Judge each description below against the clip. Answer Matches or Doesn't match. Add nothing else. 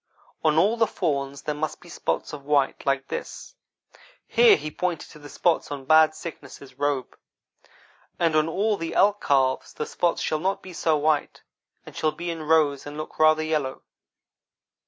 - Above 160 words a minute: Matches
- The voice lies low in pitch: Doesn't match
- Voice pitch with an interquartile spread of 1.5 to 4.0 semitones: Matches